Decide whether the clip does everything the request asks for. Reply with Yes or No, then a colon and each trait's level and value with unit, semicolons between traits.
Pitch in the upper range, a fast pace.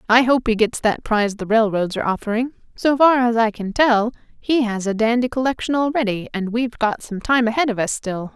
Yes: high, 230 Hz; fast, 225 wpm